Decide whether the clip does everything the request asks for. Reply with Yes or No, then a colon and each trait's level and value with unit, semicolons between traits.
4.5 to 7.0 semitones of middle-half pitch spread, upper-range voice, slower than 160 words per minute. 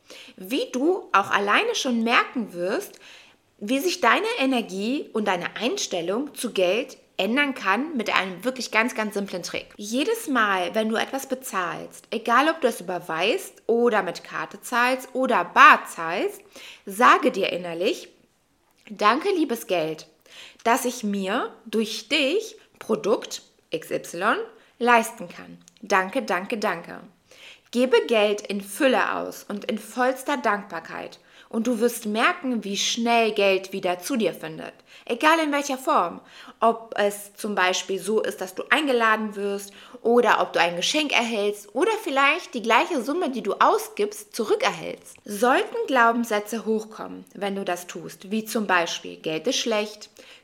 Yes: average, 4.9 semitones; high, 235 Hz; average, 145 wpm